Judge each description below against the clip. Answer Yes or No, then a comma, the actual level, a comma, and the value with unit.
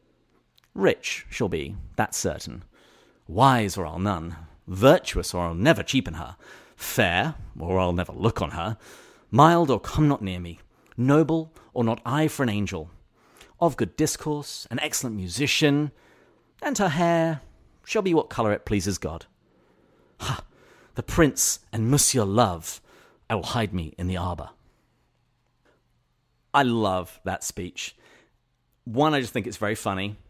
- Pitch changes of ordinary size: No, wide, 7.5 semitones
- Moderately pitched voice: No, low, 115 Hz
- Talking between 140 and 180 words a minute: Yes, average, 150 wpm